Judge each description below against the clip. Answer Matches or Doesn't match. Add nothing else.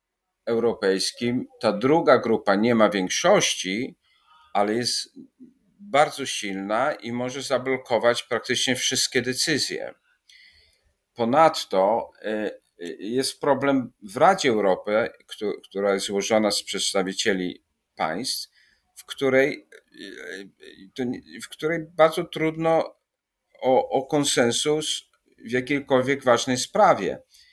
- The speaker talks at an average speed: Doesn't match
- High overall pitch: Doesn't match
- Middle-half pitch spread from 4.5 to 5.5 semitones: Matches